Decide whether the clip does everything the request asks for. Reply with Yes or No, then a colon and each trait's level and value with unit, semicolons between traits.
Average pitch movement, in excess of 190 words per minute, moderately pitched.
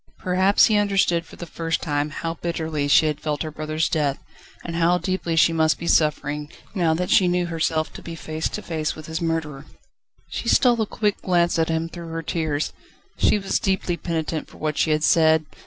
No: narrow, 1.9 semitones; fast, 205 wpm; medium, 165 Hz